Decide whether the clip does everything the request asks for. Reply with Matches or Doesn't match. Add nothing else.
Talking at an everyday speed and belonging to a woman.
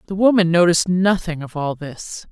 Matches